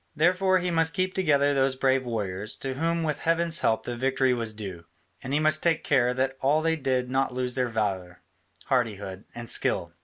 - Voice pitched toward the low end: Yes, low, 130 Hz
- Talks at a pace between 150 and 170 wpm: No, average, 195 wpm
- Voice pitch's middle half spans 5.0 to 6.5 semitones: Yes, average, 5.3 semitones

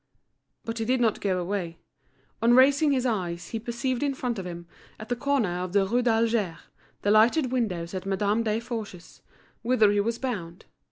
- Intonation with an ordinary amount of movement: Yes, average, 4.2 semitones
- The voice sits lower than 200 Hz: No, high, 225 Hz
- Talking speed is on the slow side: No, average, 180 wpm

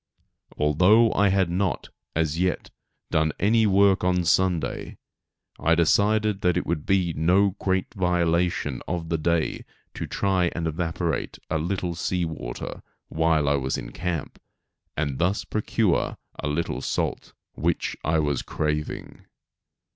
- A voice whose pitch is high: No, very low, 85 Hz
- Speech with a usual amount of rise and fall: Yes, average, 3.1 semitones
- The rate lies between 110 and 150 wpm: Yes, average, 140 wpm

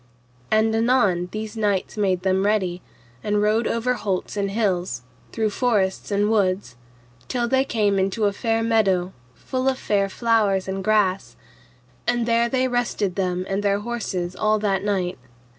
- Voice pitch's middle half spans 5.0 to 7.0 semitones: No, average, 3.0 semitones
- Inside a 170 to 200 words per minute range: No, average, 160 wpm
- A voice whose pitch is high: Yes, high, 205 Hz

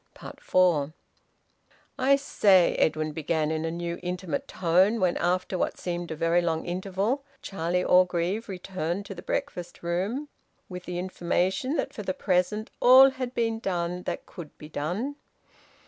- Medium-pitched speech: Yes, medium, 180 Hz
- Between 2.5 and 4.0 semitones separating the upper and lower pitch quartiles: Yes, average, 2.9 semitones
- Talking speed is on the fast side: No, average, 150 wpm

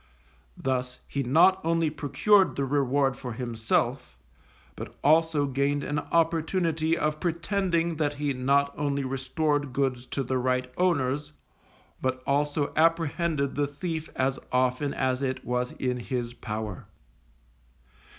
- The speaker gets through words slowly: Yes, slow, 130 wpm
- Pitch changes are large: No, average, 3.6 semitones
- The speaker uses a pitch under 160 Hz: Yes, medium, 140 Hz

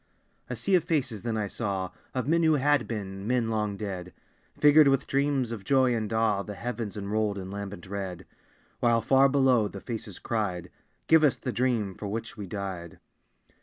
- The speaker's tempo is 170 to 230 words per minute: Yes, average, 185 wpm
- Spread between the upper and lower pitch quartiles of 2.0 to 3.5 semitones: No, average, 4.7 semitones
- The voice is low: Yes, low, 110 Hz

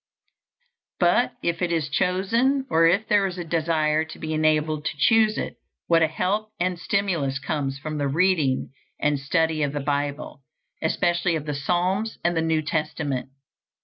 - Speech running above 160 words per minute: Yes, average, 170 wpm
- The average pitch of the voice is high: No, medium, 160 Hz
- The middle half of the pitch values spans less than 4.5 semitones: Yes, average, 3.4 semitones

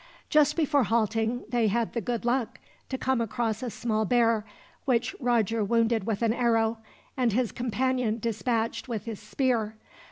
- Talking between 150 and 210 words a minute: Yes, average, 160 wpm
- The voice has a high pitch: Yes, high, 230 Hz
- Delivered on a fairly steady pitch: Yes, narrow, 1.8 semitones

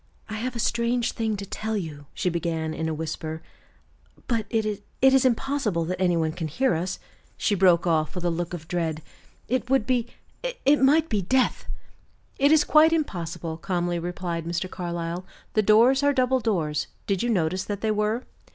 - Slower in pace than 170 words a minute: No, average, 185 wpm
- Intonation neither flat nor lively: No, wide, 6.2 semitones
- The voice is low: No, high, 195 Hz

